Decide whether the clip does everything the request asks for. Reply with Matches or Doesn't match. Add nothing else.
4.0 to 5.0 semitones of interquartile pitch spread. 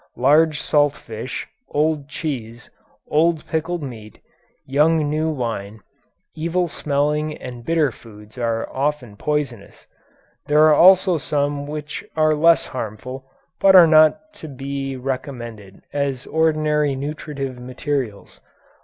Doesn't match